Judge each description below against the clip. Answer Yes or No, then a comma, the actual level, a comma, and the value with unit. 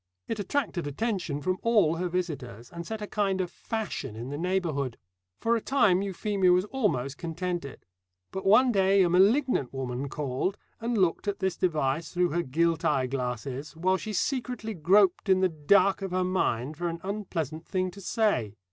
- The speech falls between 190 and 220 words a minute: No, average, 180 wpm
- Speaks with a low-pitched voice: No, medium, 180 Hz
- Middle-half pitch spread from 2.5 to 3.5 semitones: No, average, 5.0 semitones